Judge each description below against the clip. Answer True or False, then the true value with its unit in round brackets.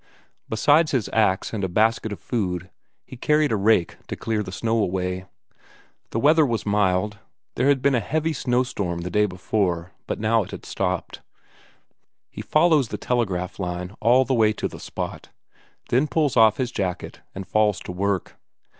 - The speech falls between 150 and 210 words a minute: True (175 wpm)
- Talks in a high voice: False (110 Hz)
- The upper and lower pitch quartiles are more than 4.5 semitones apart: True (5.0 semitones)